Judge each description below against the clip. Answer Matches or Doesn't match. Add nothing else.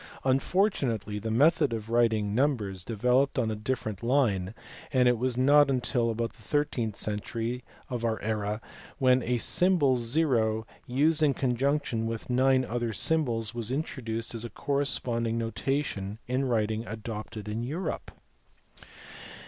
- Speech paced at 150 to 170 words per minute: Doesn't match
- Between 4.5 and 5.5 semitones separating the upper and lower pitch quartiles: Doesn't match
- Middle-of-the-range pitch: Doesn't match